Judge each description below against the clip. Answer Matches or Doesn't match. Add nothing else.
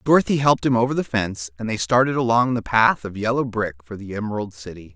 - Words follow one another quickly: Matches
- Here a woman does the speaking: Doesn't match